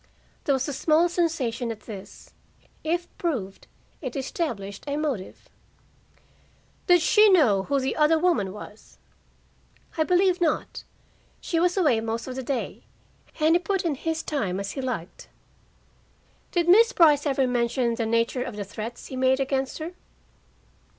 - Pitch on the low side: No, very high, 270 Hz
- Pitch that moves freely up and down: Yes, wide, 6.2 semitones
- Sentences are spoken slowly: No, average, 155 wpm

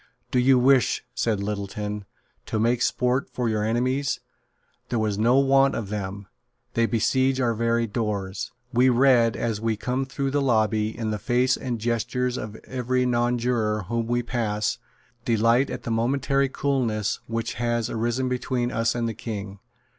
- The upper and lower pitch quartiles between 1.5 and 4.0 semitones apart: Yes, narrow, 2.5 semitones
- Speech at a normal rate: Yes, average, 160 wpm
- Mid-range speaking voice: No, low, 120 Hz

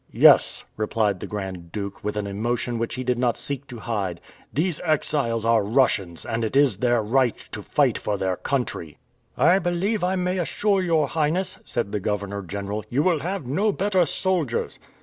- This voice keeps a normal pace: Yes, average, 185 wpm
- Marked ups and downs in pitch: Yes, wide, 7.7 semitones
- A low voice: Yes, low, 120 Hz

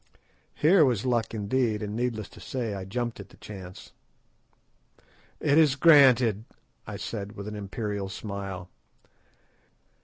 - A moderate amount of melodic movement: Yes, average, 3.9 semitones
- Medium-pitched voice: No, low, 110 Hz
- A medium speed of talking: No, slow, 130 wpm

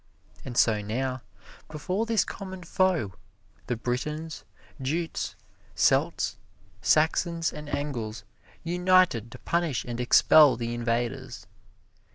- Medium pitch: Yes, medium, 145 Hz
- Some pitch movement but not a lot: No, wide, 6.2 semitones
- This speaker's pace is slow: Yes, slow, 105 wpm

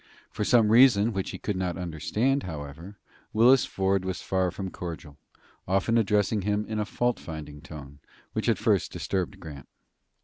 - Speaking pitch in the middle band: No, very low, 95 Hz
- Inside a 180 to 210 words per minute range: No, average, 165 wpm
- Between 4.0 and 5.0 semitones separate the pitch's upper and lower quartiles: Yes, average, 4.5 semitones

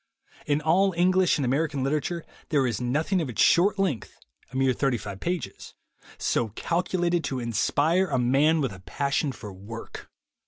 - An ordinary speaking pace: Yes, average, 175 wpm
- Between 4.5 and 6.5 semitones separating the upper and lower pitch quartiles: Yes, wide, 5.6 semitones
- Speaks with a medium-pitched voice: Yes, medium, 145 Hz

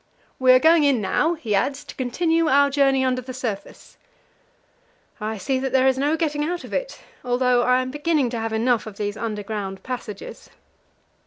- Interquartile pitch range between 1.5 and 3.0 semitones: No, average, 4.2 semitones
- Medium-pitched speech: No, very high, 255 Hz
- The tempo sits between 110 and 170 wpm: No, average, 185 wpm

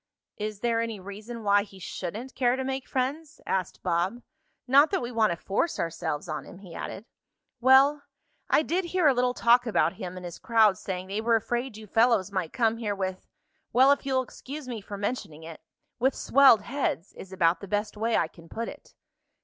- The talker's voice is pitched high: Yes, high, 220 Hz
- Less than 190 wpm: No, fast, 205 wpm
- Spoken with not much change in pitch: No, average, 5.0 semitones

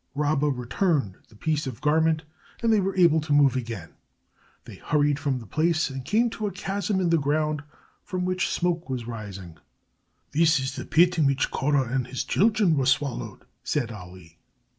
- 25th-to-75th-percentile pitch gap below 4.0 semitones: No, average, 4.8 semitones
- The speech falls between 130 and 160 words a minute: No, average, 185 wpm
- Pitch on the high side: No, medium, 150 Hz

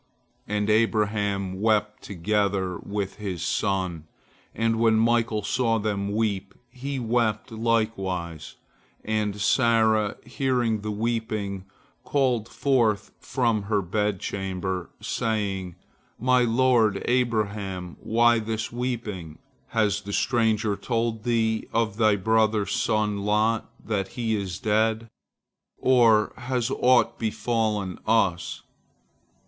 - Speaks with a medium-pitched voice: No, low, 110 Hz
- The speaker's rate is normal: No, slow, 105 wpm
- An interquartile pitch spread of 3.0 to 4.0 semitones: No, narrow, 2.4 semitones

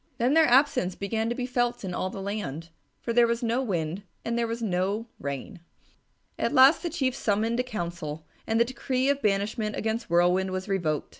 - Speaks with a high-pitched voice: Yes, high, 220 Hz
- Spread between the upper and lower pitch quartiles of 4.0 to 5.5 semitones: Yes, average, 4.5 semitones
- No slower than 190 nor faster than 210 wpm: Yes, average, 200 wpm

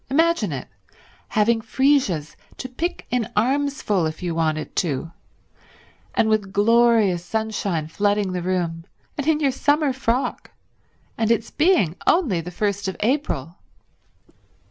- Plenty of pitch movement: Yes, wide, 7.0 semitones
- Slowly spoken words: Yes, slow, 130 wpm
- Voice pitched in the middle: No, high, 215 Hz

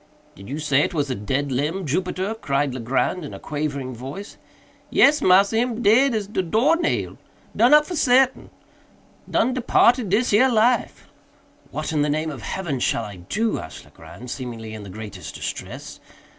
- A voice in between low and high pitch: Yes, medium, 160 Hz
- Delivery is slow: No, average, 165 wpm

